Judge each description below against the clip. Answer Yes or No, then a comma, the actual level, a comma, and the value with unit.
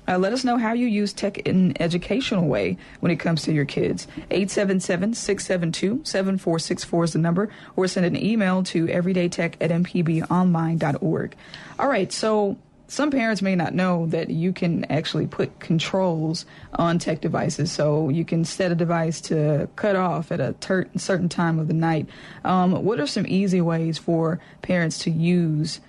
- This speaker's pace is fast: No, average, 175 wpm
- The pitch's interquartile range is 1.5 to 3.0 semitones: Yes, narrow, 2.6 semitones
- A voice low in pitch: No, medium, 175 Hz